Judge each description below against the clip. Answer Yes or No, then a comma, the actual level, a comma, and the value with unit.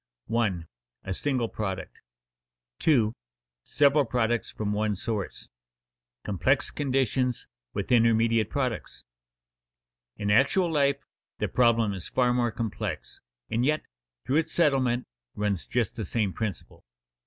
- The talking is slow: Yes, slow, 125 wpm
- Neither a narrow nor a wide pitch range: Yes, average, 3.8 semitones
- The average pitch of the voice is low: Yes, low, 115 Hz